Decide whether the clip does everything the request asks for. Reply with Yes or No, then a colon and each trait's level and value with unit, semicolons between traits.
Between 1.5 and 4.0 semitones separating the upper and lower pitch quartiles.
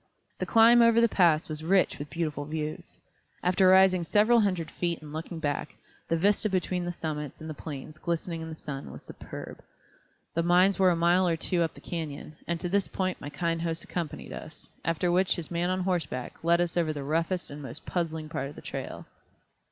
Yes: average, 2.8 semitones